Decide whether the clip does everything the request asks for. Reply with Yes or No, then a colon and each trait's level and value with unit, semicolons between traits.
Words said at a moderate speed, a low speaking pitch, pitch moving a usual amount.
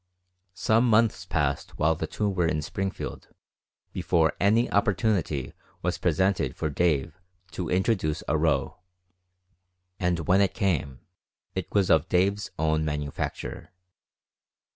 No: slow, 120 wpm; very low, 90 Hz; average, 4.2 semitones